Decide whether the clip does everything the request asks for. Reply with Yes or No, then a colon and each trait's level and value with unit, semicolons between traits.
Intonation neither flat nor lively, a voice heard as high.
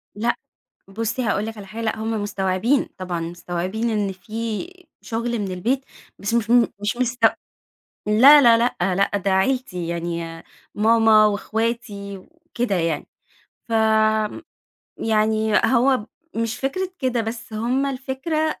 Yes: average, 3.1 semitones; high, 220 Hz